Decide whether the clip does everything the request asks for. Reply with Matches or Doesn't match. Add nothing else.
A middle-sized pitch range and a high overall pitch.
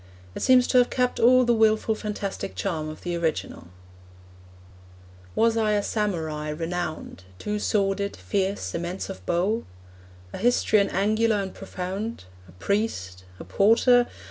Matches